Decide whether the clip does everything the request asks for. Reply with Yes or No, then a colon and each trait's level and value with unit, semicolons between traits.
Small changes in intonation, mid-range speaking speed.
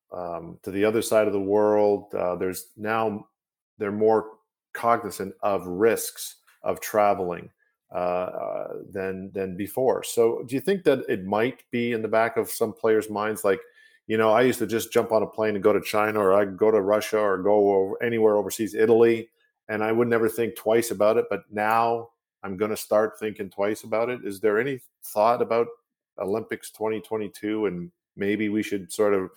Yes: narrow, 2.0 semitones; average, 195 wpm